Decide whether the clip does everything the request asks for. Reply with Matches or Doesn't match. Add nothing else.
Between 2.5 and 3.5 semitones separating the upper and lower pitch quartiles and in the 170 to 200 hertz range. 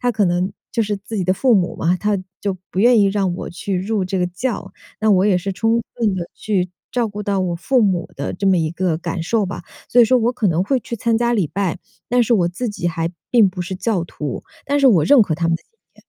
Doesn't match